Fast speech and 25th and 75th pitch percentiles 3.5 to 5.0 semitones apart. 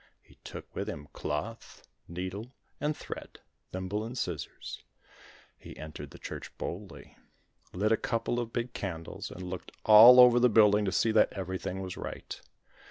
No: average, 160 wpm; average, 4.0 semitones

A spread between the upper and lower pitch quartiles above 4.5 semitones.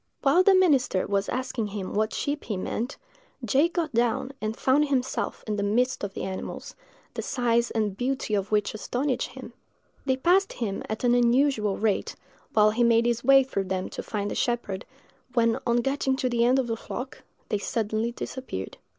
No: average, 3.8 semitones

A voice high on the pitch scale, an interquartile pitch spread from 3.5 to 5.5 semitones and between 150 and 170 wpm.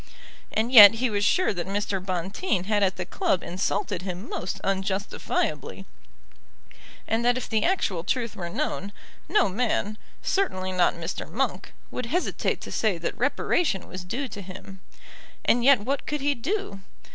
Yes: high, 205 Hz; average, 4.8 semitones; average, 160 wpm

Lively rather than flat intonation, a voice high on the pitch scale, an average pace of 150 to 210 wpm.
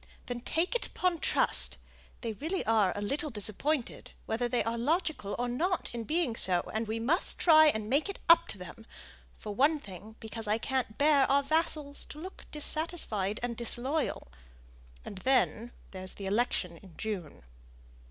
Yes: wide, 6.2 semitones; high, 240 Hz; average, 170 wpm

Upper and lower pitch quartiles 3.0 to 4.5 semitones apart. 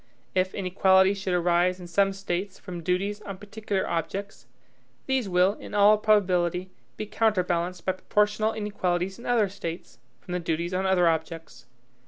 No: narrow, 2.5 semitones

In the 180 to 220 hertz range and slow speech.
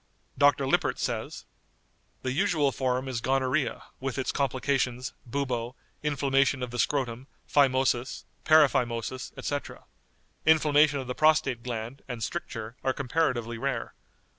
No: low, 130 Hz; slow, 120 wpm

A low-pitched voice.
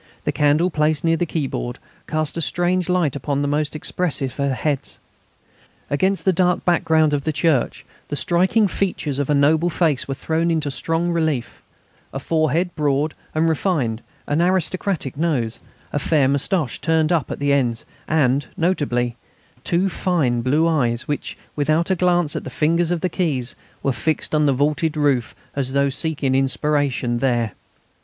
No: medium, 150 Hz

